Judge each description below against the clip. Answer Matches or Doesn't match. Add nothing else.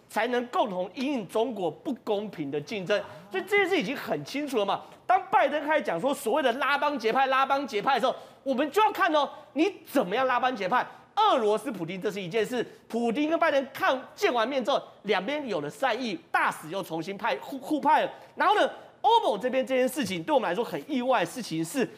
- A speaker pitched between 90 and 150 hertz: Doesn't match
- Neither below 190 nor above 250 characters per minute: Doesn't match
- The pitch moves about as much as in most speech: Doesn't match